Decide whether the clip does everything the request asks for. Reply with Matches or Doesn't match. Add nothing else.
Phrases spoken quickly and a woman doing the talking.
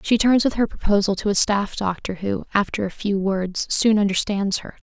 Matches